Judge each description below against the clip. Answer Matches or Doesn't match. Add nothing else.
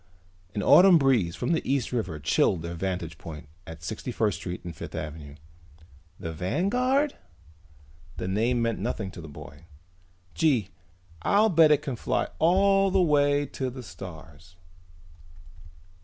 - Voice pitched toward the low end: Matches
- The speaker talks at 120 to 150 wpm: Matches